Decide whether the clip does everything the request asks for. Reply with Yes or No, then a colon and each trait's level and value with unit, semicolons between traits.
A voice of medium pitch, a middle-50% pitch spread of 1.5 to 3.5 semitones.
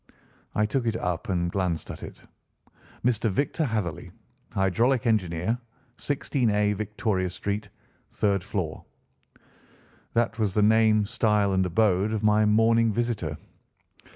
No: low, 105 Hz; average, 3.1 semitones